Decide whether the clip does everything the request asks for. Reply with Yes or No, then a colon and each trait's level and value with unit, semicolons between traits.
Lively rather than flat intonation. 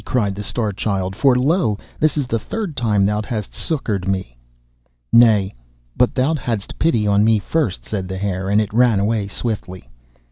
No: average, 4.0 semitones